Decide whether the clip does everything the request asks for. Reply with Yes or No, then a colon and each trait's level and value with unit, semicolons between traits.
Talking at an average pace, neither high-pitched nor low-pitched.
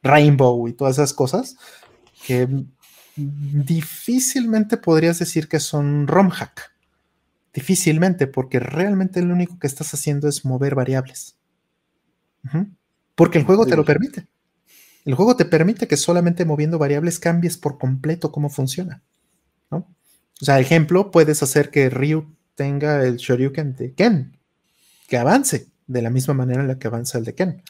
Yes: average, 150 wpm; medium, 150 Hz